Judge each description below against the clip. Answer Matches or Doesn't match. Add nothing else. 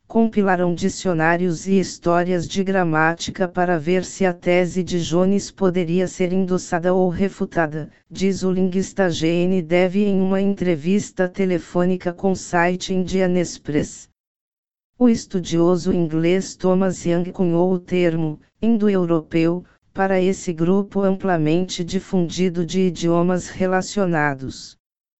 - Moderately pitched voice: Matches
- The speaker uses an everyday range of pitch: Doesn't match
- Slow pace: Matches